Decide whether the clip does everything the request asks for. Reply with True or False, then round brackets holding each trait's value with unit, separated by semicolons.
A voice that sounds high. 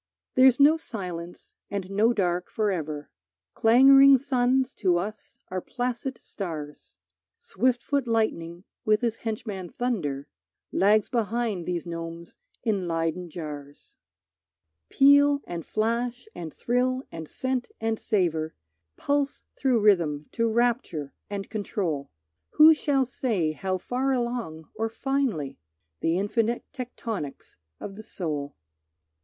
True (215 Hz)